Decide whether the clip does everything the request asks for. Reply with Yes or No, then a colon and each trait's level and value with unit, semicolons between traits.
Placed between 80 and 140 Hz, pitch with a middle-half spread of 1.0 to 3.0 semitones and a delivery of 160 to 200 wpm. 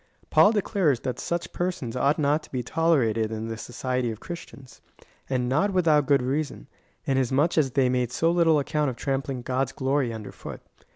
No: low, 135 Hz; average, 3.9 semitones; average, 180 wpm